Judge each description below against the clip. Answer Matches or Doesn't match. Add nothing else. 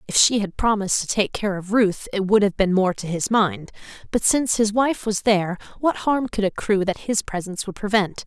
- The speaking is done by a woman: Matches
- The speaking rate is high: Matches